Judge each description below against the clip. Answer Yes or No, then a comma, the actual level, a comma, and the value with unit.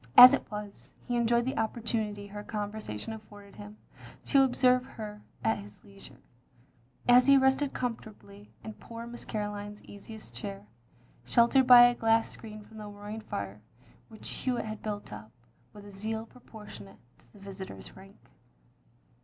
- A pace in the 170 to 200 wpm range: No, average, 155 wpm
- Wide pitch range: No, narrow, 2.5 semitones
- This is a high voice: Yes, high, 215 Hz